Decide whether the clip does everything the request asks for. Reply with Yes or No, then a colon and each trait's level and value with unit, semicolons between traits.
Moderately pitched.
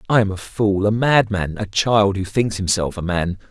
No: low, 100 Hz